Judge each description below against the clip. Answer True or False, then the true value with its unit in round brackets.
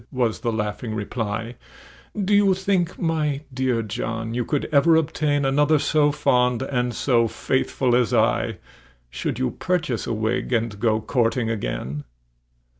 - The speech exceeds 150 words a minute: False (145 wpm)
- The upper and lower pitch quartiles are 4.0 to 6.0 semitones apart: True (4.7 semitones)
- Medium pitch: False (125 Hz)